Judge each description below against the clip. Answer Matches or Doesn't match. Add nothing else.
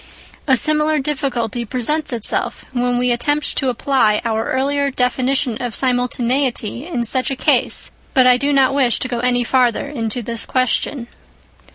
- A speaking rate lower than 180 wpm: Matches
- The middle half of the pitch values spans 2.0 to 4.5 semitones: Matches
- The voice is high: Matches